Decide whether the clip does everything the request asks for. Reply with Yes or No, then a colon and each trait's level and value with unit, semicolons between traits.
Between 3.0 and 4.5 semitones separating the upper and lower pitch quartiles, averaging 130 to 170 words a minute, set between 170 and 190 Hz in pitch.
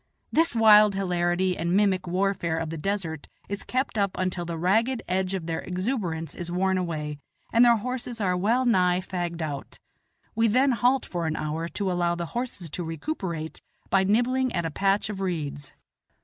No: average, 4.0 semitones; average, 180 wpm; medium, 185 Hz